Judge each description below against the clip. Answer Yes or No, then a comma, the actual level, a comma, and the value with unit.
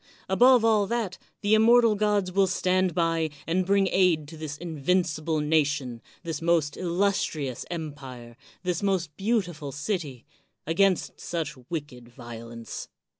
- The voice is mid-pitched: Yes, medium, 170 Hz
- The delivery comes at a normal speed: No, slow, 130 wpm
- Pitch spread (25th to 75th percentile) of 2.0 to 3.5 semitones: No, average, 4.7 semitones